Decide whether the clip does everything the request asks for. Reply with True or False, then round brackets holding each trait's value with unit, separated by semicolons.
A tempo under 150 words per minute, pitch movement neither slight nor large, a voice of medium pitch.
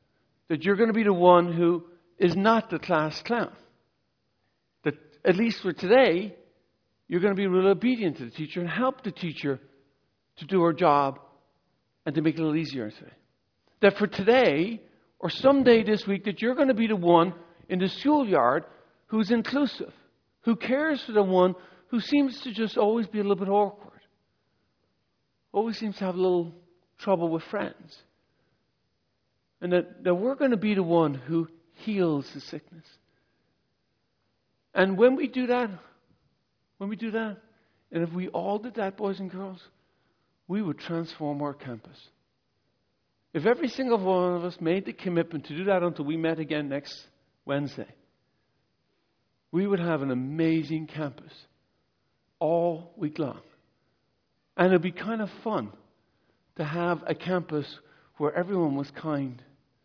False (165 wpm; 4.8 semitones; 180 Hz)